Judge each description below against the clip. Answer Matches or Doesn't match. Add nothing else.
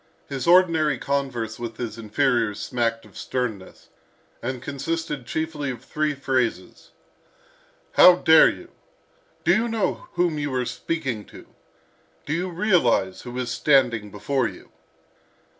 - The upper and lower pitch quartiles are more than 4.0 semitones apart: Matches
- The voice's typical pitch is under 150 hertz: Matches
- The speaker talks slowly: Matches